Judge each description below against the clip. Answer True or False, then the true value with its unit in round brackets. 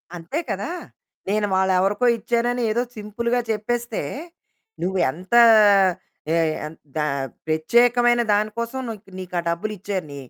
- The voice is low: False (210 Hz)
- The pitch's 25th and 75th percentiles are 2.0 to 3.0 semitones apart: False (4.3 semitones)